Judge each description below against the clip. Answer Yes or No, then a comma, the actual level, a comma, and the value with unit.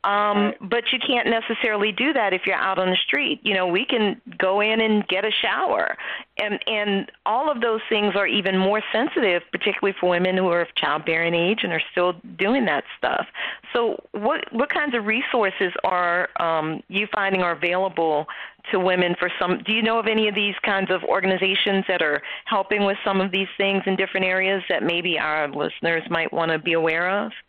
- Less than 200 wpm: No, fast, 205 wpm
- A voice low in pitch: No, high, 195 Hz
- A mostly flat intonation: No, average, 3.1 semitones